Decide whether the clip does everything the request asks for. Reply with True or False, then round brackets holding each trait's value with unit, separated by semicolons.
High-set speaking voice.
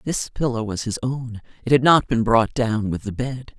False (120 Hz)